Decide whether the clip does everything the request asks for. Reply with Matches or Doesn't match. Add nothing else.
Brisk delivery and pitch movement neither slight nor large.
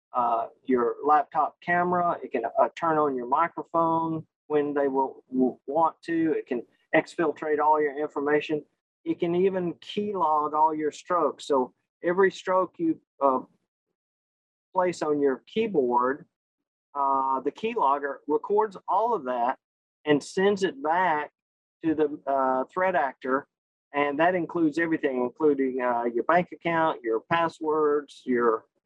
Doesn't match